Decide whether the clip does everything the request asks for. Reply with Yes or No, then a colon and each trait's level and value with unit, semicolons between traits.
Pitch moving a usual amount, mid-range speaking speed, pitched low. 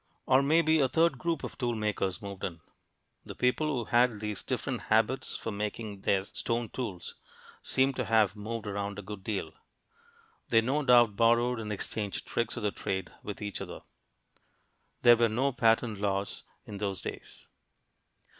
Yes: average, 3.4 semitones; average, 165 wpm; low, 110 Hz